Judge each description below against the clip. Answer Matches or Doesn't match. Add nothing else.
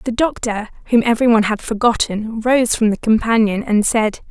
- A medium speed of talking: Matches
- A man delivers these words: Doesn't match